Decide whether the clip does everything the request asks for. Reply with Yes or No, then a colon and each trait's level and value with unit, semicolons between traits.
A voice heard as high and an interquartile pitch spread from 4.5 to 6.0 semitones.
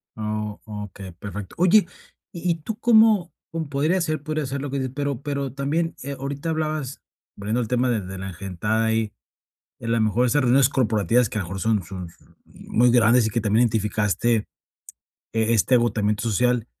No: low, 120 Hz; average, 5.0 semitones